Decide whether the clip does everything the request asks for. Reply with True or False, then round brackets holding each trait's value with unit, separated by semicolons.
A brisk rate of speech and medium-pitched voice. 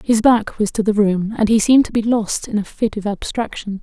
False (265 wpm; 215 Hz)